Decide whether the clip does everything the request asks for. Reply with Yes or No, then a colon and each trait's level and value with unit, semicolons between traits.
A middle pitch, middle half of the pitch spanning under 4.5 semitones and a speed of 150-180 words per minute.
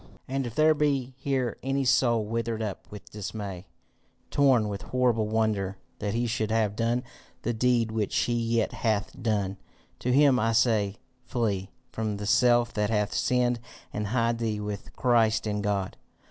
No: low, 115 Hz; average, 2.8 semitones; average, 165 wpm